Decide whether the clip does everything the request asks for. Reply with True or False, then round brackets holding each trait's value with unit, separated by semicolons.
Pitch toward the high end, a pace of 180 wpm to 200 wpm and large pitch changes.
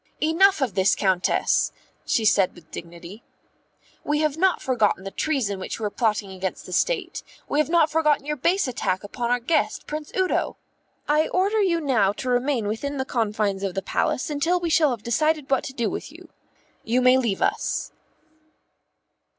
True (255 Hz; 185 wpm; 7.1 semitones)